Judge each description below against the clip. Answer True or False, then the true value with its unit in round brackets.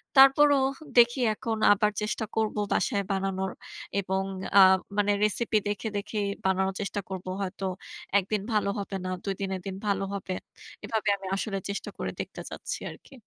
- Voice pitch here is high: True (200 Hz)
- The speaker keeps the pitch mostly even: True (2.2 semitones)